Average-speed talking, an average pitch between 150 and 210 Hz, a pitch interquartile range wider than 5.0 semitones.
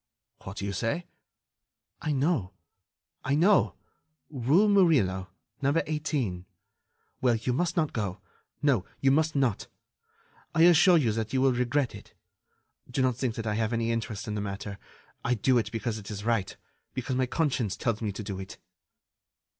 No: average, 170 wpm; low, 120 Hz; wide, 5.4 semitones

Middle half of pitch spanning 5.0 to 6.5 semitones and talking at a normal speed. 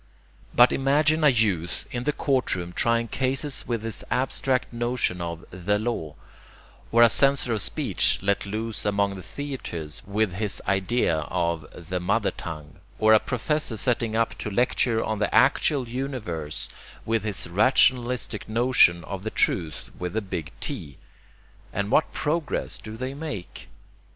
Yes: wide, 5.4 semitones; average, 150 wpm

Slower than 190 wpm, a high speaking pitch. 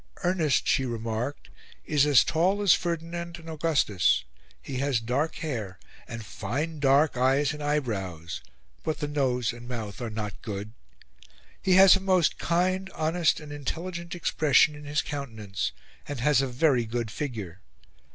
No: average, 150 wpm; medium, 140 Hz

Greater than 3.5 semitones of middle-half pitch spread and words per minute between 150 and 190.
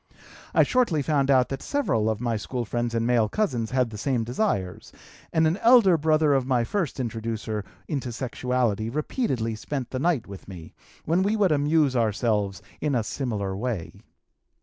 Yes: wide, 5.4 semitones; average, 170 wpm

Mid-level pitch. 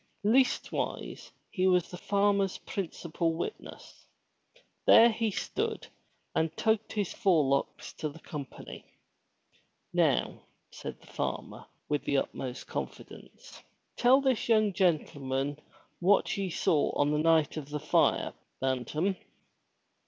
Yes: medium, 175 Hz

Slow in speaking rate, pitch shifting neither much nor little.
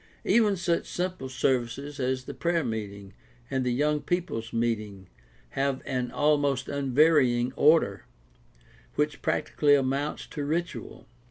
Yes: slow, 120 wpm; average, 3.6 semitones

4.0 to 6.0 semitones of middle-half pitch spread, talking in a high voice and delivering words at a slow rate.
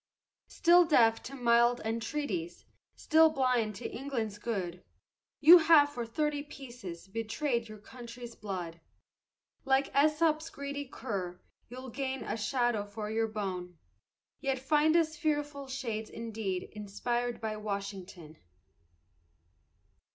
Yes: average, 5.1 semitones; high, 235 Hz; slow, 115 wpm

